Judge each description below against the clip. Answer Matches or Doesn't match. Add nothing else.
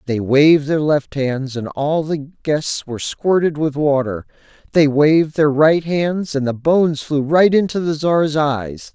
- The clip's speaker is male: Matches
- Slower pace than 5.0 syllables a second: Matches